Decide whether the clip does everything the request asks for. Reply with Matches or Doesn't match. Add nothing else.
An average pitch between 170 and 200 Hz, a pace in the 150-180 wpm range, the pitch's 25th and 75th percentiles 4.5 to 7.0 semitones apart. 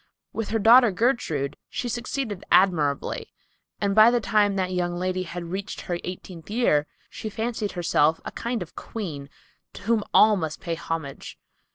Matches